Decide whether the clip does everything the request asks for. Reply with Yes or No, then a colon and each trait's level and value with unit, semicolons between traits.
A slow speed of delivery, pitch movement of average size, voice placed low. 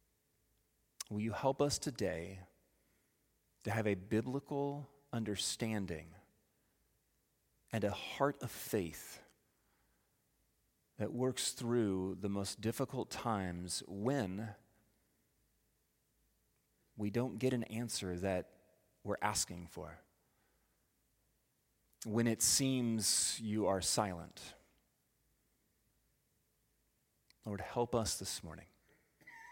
Yes: slow, 85 wpm; average, 4.1 semitones; low, 110 Hz